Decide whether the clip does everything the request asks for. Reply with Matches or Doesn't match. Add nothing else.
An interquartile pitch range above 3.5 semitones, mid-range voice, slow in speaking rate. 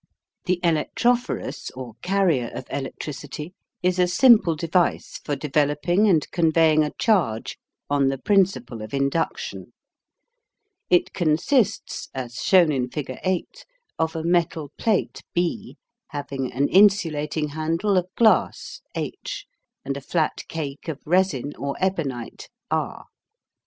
Matches